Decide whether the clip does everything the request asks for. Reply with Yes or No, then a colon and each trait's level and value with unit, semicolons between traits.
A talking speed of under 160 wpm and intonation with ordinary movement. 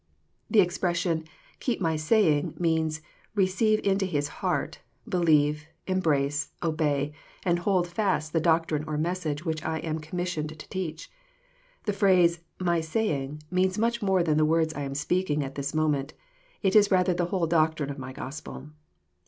No: average, 175 wpm; average, 3.5 semitones